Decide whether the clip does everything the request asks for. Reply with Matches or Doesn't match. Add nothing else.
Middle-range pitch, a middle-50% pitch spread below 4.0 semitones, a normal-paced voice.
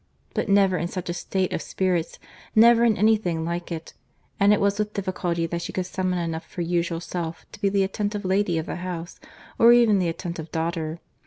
Doesn't match